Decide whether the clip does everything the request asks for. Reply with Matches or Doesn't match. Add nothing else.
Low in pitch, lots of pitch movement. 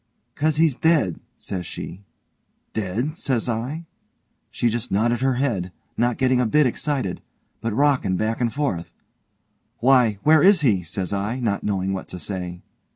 Matches